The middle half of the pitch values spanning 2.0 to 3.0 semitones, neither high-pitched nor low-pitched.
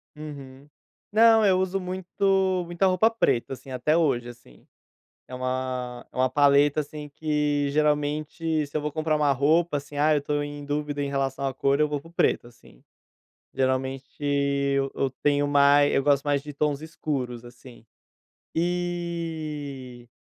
Yes: narrow, 2.5 semitones; medium, 145 Hz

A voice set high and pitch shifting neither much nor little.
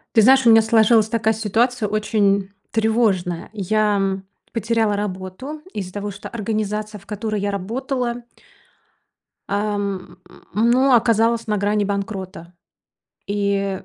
No: high, 210 Hz; narrow, 2.2 semitones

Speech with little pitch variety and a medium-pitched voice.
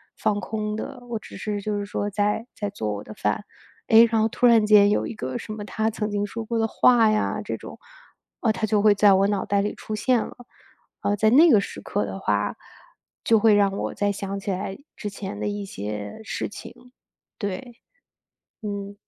No: narrow, 1.6 semitones; high, 205 Hz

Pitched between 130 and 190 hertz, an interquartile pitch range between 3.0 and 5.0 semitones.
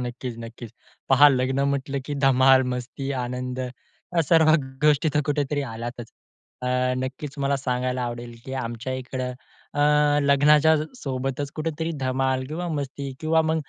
No: low, 135 Hz; narrow, 2.5 semitones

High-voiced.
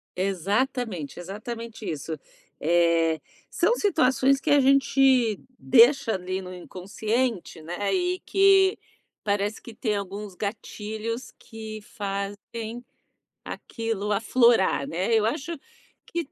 Yes: high, 220 Hz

